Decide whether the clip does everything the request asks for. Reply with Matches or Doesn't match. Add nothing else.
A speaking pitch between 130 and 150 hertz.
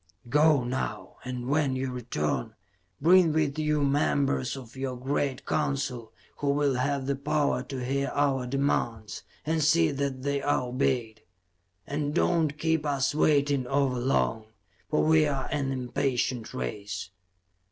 Matches